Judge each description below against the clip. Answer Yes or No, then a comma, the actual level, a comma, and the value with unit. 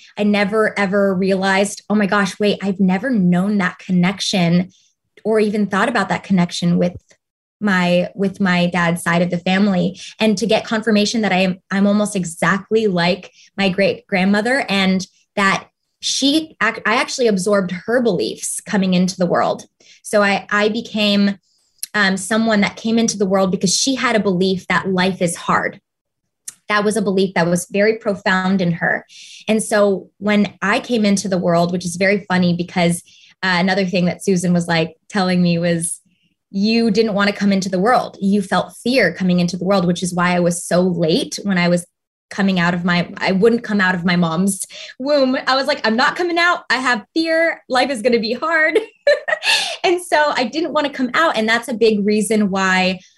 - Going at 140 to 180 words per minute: No, average, 195 wpm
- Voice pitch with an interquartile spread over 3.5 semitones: No, average, 3.2 semitones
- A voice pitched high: Yes, high, 200 Hz